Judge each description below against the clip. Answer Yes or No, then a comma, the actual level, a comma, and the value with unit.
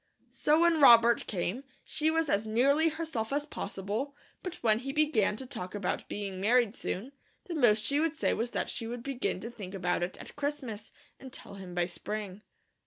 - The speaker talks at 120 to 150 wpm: No, average, 195 wpm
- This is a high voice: Yes, high, 235 Hz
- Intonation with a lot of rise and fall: Yes, wide, 5.9 semitones